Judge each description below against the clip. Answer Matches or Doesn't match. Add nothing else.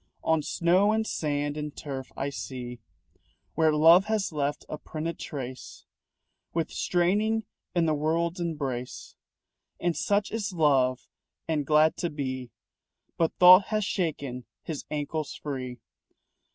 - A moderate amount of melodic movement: Matches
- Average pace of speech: Doesn't match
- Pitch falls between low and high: Matches